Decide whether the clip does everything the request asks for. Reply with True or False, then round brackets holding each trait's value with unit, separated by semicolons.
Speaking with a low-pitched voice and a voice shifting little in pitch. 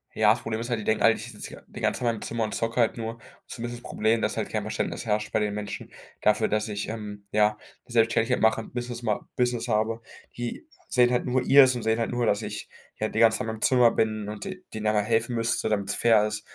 True (110 Hz; 1.9 semitones)